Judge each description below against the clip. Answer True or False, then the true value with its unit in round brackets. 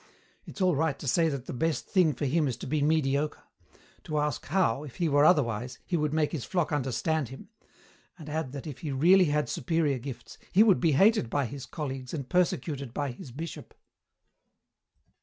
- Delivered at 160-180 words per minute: False (195 wpm)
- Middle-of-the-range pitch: True (150 Hz)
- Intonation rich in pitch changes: False (3.3 semitones)